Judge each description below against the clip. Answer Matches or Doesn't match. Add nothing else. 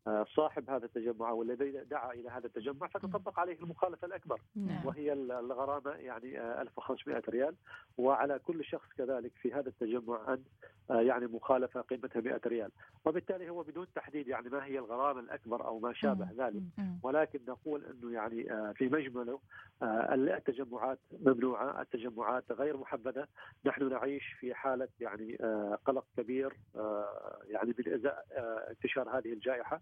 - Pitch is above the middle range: Doesn't match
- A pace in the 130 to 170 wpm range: Matches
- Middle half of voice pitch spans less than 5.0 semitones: Matches